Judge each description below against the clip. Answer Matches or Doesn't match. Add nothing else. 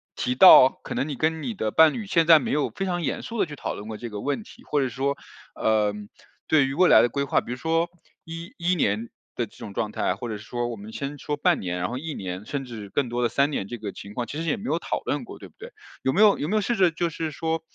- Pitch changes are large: Matches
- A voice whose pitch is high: Doesn't match